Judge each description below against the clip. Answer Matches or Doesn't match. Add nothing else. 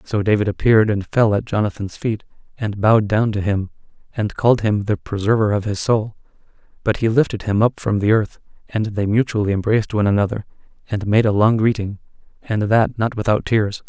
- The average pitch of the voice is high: Doesn't match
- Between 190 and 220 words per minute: Matches